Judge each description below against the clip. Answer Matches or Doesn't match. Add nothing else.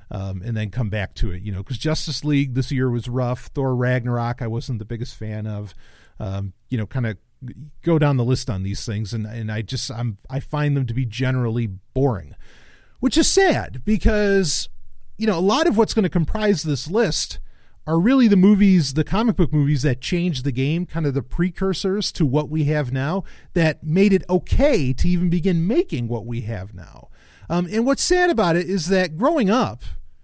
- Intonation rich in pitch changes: Matches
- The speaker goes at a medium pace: Doesn't match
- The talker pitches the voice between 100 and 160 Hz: Matches